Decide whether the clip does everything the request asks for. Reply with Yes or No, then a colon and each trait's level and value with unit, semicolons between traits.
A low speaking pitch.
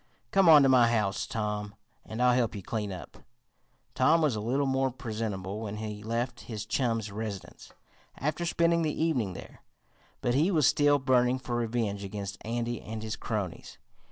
Yes: low, 115 Hz